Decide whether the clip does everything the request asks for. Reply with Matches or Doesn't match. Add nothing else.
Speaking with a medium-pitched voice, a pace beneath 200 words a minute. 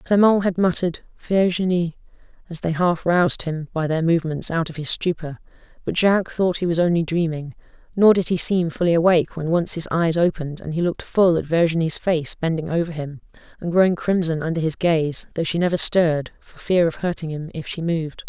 Doesn't match